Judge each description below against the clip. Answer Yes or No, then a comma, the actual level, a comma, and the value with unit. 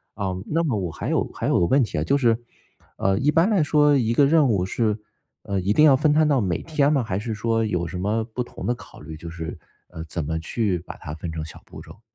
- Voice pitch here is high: No, low, 110 Hz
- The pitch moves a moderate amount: No, wide, 7.7 semitones